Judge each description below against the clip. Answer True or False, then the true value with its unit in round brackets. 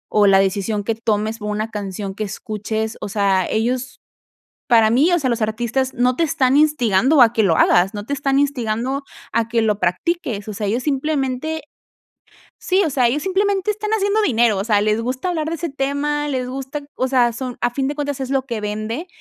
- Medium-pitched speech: False (245 Hz)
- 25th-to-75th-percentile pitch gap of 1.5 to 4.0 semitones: False (4.8 semitones)